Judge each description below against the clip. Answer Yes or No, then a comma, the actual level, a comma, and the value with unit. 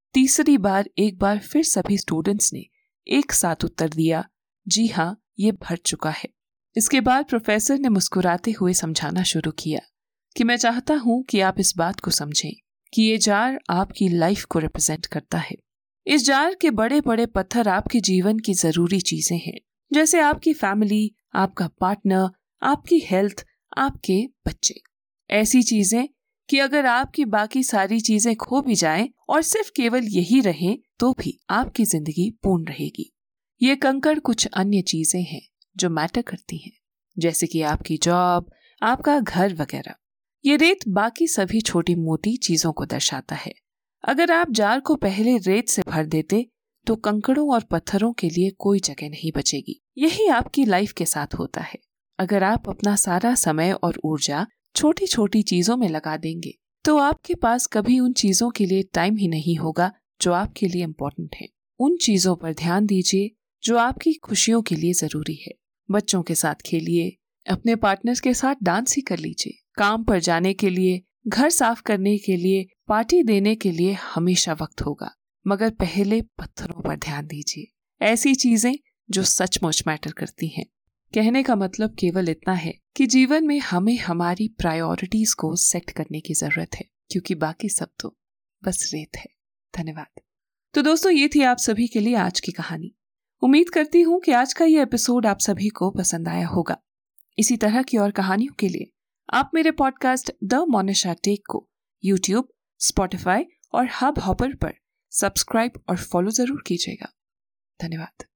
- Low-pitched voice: No, high, 205 Hz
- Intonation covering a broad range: Yes, wide, 5.7 semitones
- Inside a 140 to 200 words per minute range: Yes, average, 170 wpm